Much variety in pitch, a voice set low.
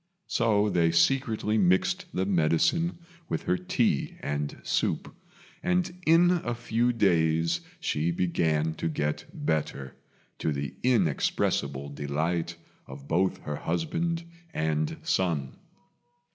Yes: wide, 7.5 semitones; very low, 85 Hz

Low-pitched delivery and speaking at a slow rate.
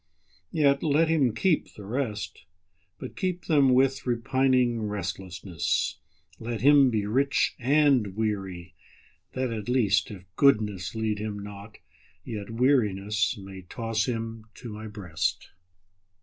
Yes: low, 110 Hz; slow, 110 wpm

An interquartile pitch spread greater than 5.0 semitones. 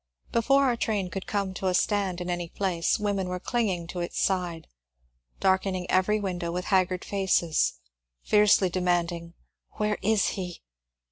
No: narrow, 2.4 semitones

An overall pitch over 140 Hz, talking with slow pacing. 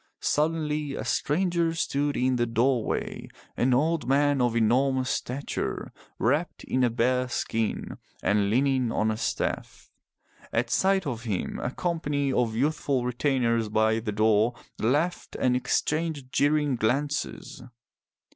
No: low, 130 Hz; slow, 130 wpm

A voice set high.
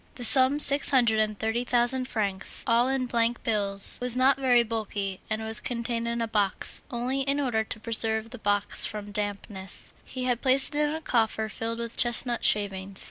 Yes: high, 230 Hz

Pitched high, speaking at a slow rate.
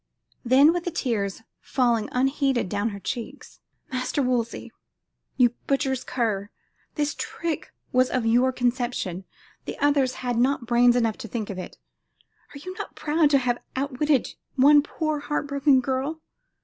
No: very high, 255 Hz; average, 150 wpm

